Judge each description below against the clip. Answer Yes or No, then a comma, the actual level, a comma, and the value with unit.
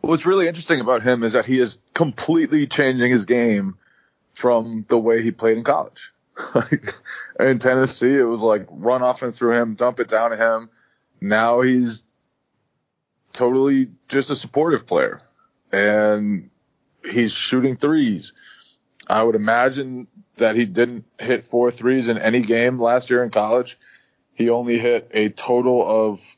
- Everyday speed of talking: Yes, average, 155 wpm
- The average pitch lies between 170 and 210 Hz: No, low, 120 Hz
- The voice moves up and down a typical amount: No, narrow, 2.0 semitones